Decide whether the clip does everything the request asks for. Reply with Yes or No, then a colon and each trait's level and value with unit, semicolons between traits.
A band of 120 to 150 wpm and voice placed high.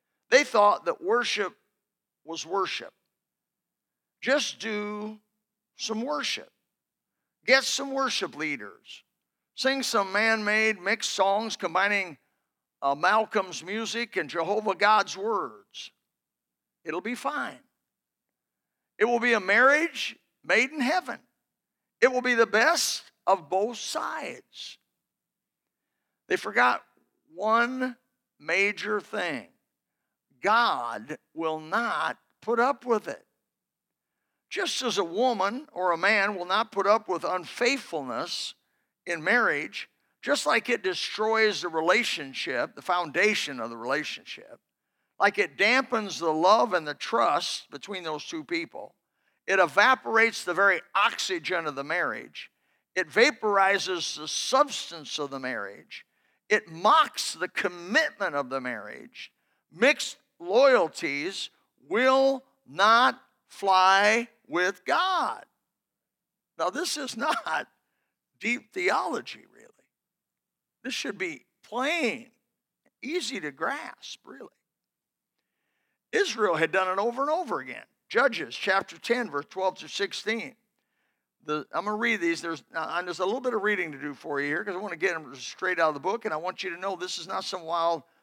Yes: slow, 135 wpm; high, 210 Hz